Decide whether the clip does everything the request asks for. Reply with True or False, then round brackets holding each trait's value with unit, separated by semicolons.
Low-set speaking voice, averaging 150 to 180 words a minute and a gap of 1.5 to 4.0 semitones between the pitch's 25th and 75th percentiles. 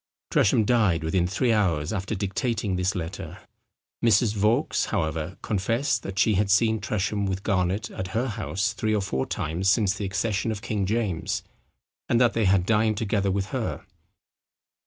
True (100 Hz; 165 wpm; 2.8 semitones)